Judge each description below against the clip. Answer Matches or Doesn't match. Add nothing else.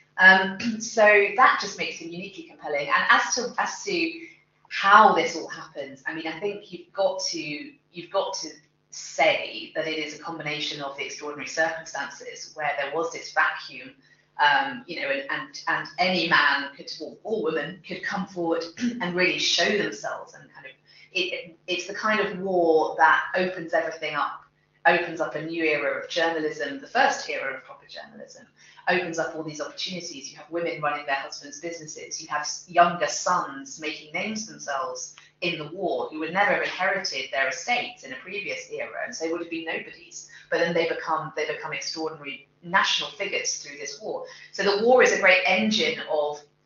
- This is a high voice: Doesn't match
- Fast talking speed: Doesn't match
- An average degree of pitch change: Matches